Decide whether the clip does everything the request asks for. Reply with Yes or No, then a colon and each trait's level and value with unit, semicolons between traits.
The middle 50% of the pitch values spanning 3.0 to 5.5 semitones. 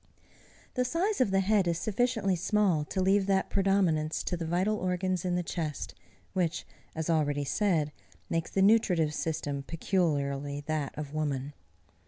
Yes: average, 4.2 semitones